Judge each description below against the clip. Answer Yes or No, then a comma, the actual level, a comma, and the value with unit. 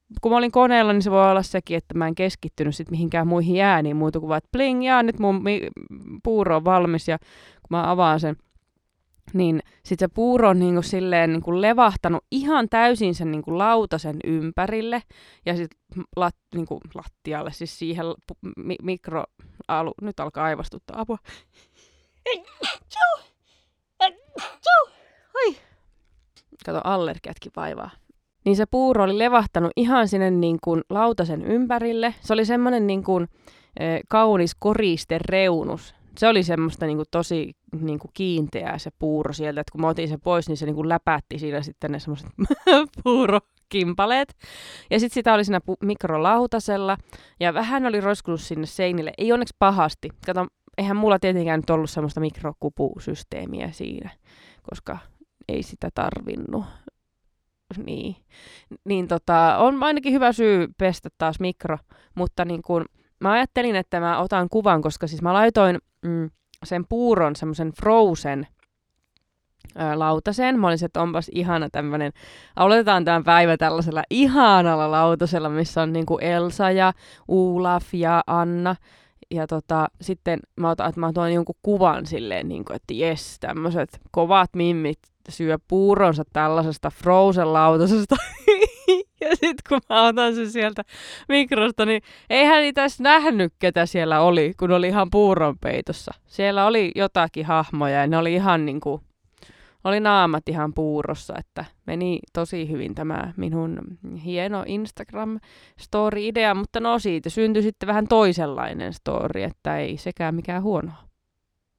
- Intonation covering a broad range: No, average, 4.7 semitones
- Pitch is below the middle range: No, medium, 180 Hz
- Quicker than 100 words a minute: Yes, average, 145 wpm